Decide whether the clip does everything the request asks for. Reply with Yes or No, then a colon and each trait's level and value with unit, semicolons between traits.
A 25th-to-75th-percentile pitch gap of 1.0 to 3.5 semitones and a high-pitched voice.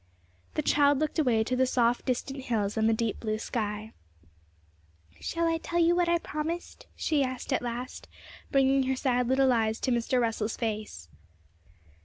No: average, 4.0 semitones; very high, 255 Hz